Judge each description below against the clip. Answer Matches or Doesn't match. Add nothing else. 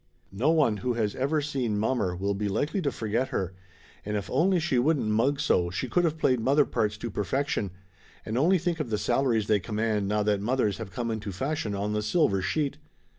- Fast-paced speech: Matches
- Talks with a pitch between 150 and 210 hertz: Doesn't match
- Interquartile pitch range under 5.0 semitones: Doesn't match